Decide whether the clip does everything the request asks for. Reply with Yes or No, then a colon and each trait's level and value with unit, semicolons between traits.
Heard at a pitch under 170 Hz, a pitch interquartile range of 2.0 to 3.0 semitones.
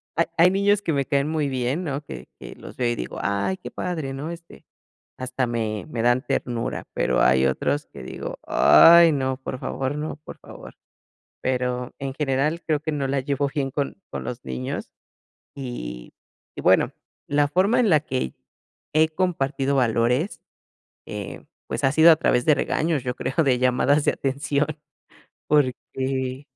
No: low, 135 Hz; average, 3.6 semitones